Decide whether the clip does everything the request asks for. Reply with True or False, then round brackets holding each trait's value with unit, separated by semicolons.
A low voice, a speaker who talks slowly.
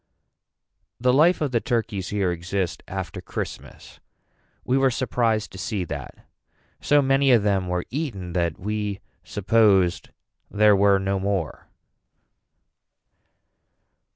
True (100 Hz; 120 wpm)